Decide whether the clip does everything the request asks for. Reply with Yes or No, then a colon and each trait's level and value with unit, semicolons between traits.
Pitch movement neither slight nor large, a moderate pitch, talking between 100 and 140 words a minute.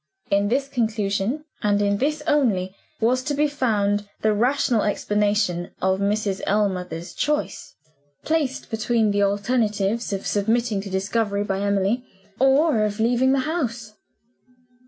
No: average, 4.0 semitones; high, 215 Hz; slow, 135 wpm